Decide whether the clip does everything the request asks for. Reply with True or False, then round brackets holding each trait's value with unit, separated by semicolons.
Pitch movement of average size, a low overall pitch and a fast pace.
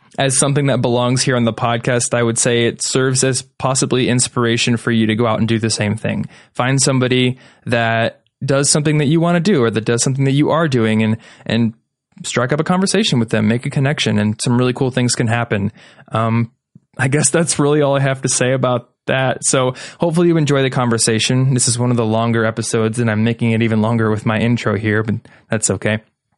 True (3.0 semitones; 125 Hz; 225 wpm)